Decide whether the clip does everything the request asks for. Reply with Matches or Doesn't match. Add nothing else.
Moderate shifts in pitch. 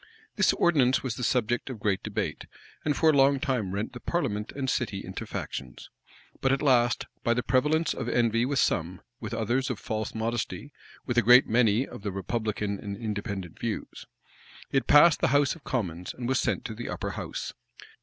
Matches